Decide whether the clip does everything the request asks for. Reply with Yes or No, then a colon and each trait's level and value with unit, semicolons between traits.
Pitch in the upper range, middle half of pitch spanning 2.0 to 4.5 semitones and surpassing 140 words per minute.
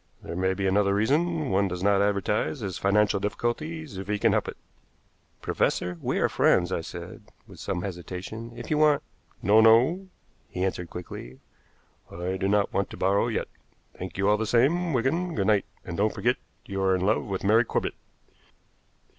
No: low, 100 Hz; average, 3.8 semitones; average, 190 wpm